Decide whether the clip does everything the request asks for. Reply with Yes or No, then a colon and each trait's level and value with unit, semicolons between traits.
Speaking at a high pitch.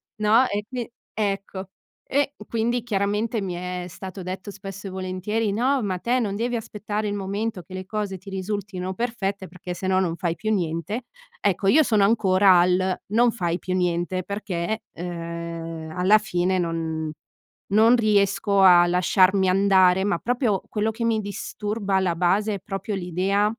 Yes: high, 195 Hz